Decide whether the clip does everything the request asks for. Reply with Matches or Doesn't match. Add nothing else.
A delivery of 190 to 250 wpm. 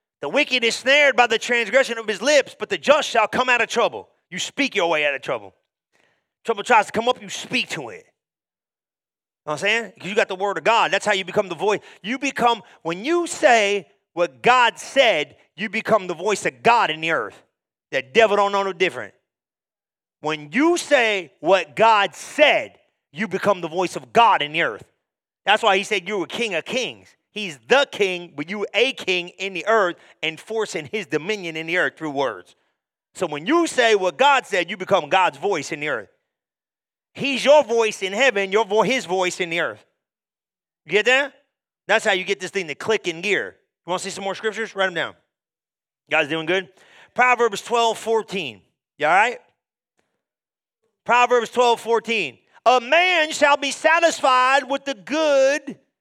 Matches